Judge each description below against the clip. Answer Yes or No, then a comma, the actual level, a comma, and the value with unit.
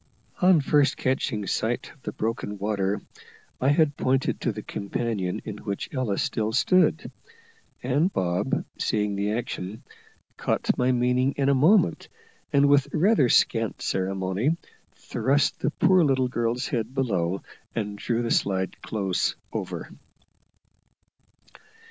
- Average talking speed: No, slow, 130 wpm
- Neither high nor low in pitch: No, low, 120 Hz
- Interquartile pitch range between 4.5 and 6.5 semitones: Yes, average, 5.3 semitones